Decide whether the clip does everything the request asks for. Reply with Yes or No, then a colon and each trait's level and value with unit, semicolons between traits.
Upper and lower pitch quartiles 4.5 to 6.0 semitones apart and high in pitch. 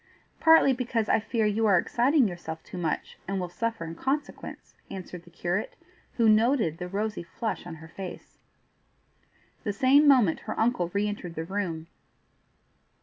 Yes: average, 5.0 semitones; high, 205 Hz